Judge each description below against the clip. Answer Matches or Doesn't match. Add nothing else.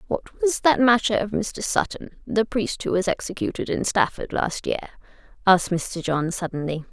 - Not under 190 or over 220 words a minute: Doesn't match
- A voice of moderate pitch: Doesn't match